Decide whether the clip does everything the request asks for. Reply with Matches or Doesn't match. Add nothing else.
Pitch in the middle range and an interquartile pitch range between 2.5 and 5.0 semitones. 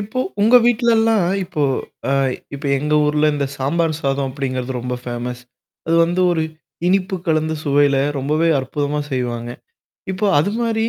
Doesn't match